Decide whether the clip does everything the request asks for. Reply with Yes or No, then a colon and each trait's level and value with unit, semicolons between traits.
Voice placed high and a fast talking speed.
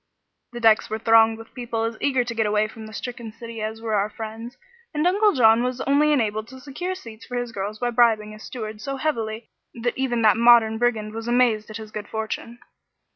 Yes: high, 230 Hz; fast, 220 wpm